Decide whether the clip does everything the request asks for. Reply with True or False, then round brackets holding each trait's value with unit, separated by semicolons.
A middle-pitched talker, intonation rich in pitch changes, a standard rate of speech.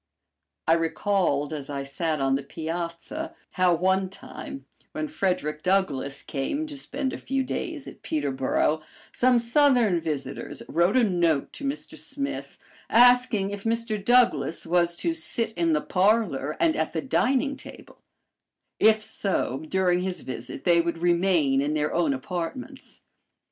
True (180 Hz; 7.6 semitones; 150 wpm)